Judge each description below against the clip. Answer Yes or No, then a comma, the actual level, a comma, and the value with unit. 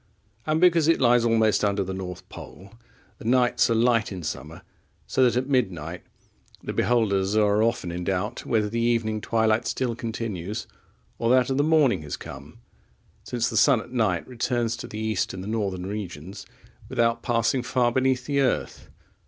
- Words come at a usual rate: Yes, average, 175 wpm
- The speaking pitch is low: Yes, low, 115 Hz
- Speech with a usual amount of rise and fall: Yes, average, 3.7 semitones